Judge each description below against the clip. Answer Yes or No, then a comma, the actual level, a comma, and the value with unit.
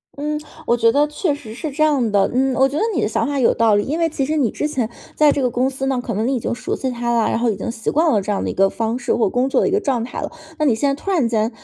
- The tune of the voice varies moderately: Yes, average, 4.0 semitones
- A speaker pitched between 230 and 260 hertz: Yes, very high, 255 Hz